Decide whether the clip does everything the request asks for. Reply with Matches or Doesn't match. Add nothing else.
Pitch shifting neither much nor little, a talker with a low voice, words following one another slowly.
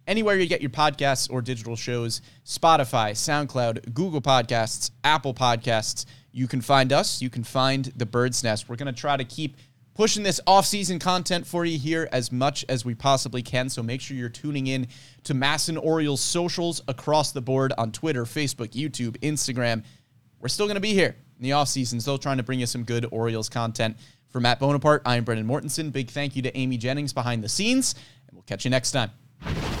Doesn't match